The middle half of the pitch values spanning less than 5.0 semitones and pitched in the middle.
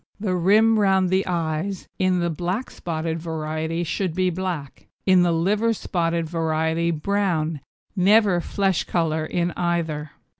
Yes: average, 2.7 semitones; medium, 175 Hz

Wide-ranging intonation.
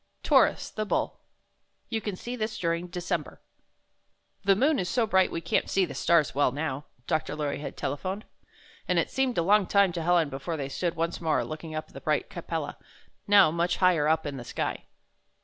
No: average, 4.0 semitones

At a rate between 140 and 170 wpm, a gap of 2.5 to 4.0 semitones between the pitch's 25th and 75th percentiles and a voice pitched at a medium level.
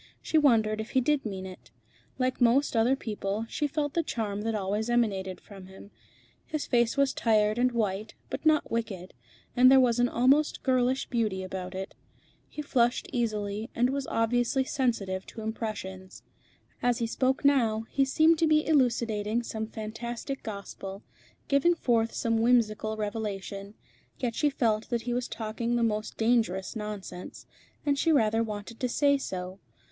No: average, 165 wpm; average, 3.4 semitones; high, 230 Hz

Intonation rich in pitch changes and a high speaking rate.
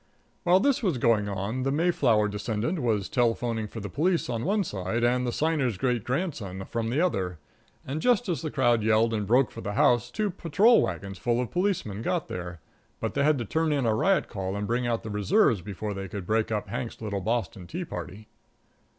Yes: wide, 6.4 semitones; fast, 210 wpm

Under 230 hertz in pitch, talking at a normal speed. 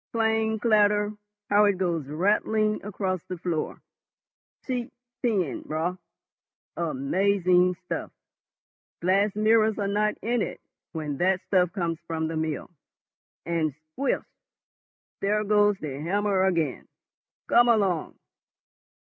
No: high, 190 Hz; slow, 105 wpm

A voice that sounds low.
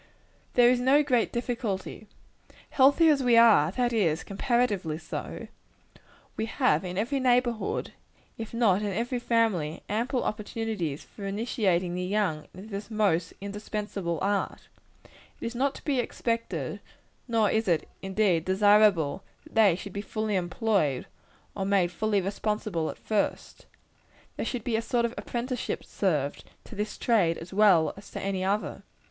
No: high, 210 Hz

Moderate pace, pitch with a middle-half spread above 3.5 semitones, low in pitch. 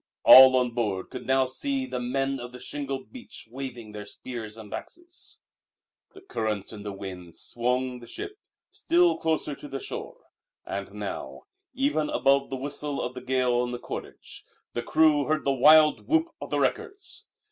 Yes: average, 175 wpm; average, 4.5 semitones; low, 130 Hz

